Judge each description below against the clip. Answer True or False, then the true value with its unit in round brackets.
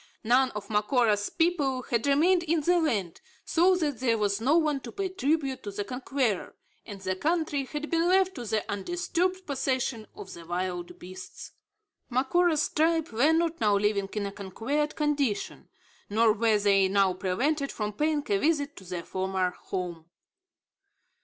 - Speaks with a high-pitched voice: True (255 Hz)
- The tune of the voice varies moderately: False (7.5 semitones)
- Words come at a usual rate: True (165 wpm)